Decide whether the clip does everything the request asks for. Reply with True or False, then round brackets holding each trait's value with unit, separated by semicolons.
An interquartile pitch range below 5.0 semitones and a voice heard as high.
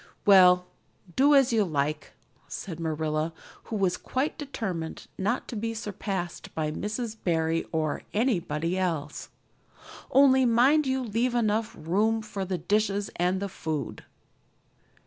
False (5.6 semitones; 195 Hz)